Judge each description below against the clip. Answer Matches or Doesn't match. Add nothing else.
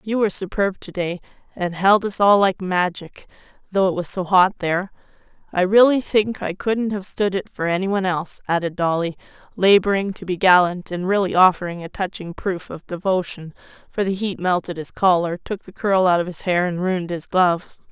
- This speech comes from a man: Doesn't match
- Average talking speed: Matches